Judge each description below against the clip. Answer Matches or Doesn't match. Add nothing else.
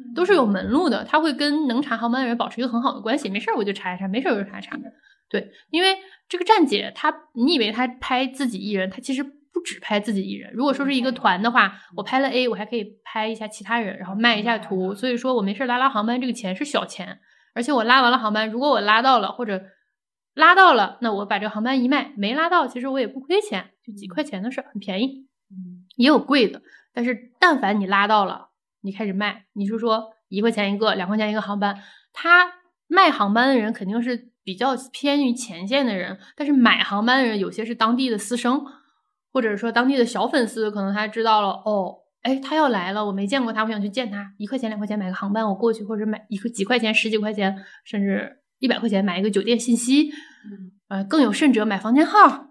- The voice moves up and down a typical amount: Matches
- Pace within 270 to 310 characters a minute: Doesn't match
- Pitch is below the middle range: Doesn't match